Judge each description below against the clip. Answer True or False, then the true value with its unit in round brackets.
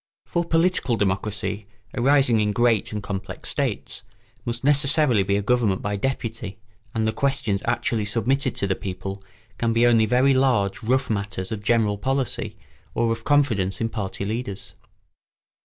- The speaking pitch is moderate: False (115 Hz)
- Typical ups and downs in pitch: True (4.0 semitones)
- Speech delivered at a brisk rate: False (155 wpm)